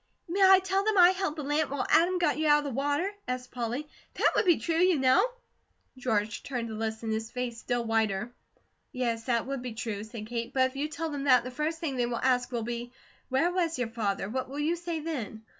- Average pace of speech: No, fast, 240 wpm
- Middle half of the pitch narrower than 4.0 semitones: No, wide, 5.4 semitones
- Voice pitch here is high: Yes, very high, 260 Hz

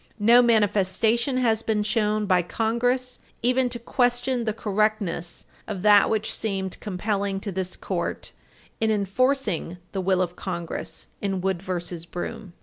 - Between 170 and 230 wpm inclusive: No, average, 145 wpm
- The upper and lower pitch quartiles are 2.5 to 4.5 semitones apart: Yes, average, 3.6 semitones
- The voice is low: No, high, 210 Hz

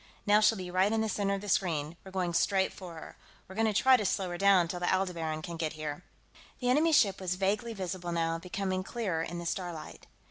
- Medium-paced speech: No, fast, 240 wpm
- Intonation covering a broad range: No, average, 2.9 semitones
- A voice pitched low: No, medium, 185 Hz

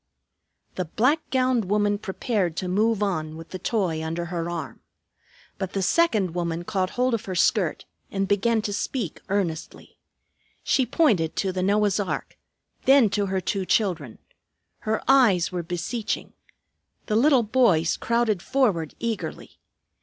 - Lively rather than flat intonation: No, average, 4.5 semitones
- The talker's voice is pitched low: No, high, 200 Hz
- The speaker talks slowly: No, average, 145 wpm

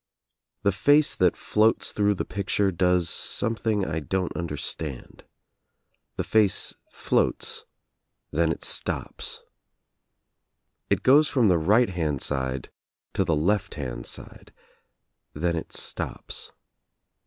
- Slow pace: Yes, slow, 115 wpm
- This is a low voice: Yes, very low, 90 Hz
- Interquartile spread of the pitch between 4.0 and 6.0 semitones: Yes, average, 4.6 semitones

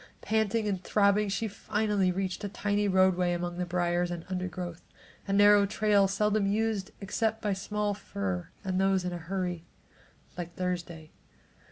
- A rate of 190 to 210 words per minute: No, average, 155 wpm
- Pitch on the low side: No, high, 195 Hz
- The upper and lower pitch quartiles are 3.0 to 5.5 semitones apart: No, narrow, 2.6 semitones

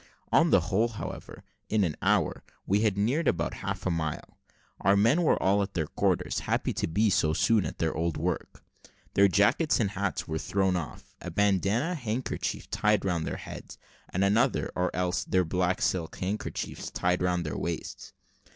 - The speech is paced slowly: No, average, 180 wpm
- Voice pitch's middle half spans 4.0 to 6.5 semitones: No, average, 3.1 semitones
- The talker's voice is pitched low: Yes, very low, 95 Hz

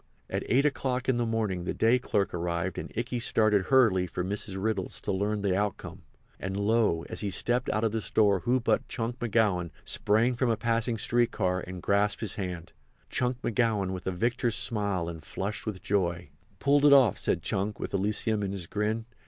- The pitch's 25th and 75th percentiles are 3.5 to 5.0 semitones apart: Yes, average, 3.8 semitones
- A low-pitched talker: Yes, low, 105 Hz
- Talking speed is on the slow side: No, average, 195 wpm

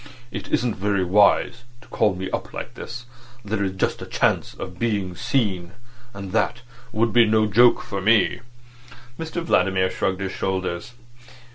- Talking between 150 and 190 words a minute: Yes, average, 160 wpm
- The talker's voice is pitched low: Yes, low, 105 Hz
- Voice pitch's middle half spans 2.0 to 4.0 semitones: Yes, average, 3.7 semitones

